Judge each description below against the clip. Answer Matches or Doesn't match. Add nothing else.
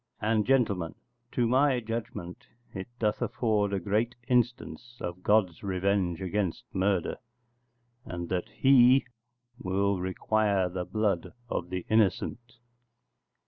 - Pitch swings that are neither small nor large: Matches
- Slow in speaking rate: Matches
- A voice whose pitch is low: Matches